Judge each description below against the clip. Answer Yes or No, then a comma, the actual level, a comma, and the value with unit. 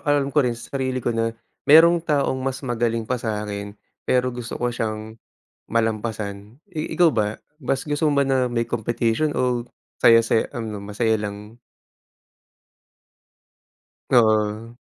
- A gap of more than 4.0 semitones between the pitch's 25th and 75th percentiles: No, average, 3.1 semitones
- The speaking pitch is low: Yes, low, 115 Hz